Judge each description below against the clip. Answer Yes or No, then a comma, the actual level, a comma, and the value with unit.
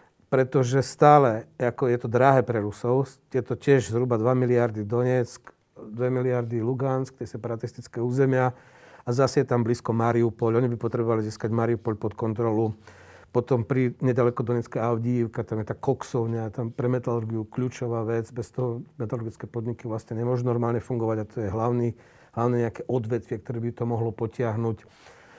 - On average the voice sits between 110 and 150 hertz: Yes, low, 120 Hz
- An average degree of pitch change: No, narrow, 1.6 semitones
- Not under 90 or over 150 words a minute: No, average, 160 wpm